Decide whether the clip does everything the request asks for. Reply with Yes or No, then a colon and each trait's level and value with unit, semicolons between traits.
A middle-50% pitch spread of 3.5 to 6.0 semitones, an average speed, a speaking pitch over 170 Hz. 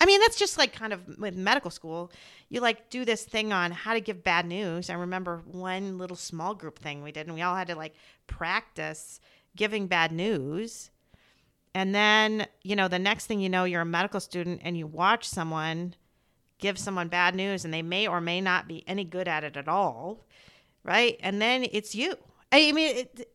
No: average, 3.8 semitones; fast, 210 wpm; medium, 185 Hz